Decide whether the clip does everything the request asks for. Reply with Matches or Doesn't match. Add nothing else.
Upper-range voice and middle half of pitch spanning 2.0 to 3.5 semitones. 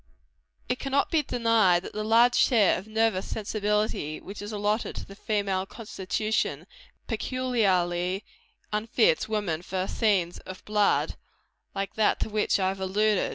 Matches